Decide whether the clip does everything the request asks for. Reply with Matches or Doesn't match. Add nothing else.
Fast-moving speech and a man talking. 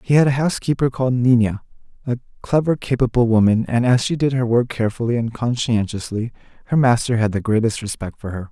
Doesn't match